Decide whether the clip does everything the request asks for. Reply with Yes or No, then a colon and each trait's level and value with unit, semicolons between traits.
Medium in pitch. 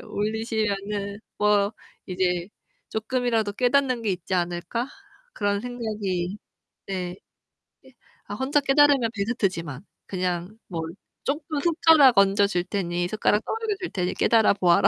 No: high, 205 Hz